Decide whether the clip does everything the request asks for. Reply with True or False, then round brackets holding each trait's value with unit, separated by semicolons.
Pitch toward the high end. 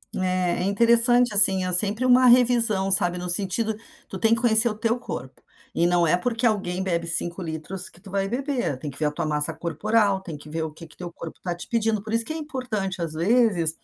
True (195 Hz)